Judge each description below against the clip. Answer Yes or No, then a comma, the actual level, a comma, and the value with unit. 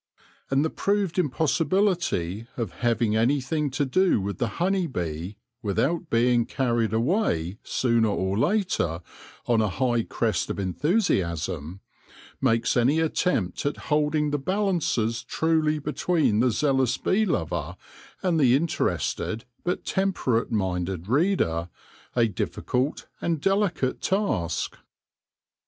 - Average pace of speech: No, slow, 120 wpm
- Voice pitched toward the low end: Yes, low, 130 Hz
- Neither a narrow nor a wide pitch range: No, wide, 7.3 semitones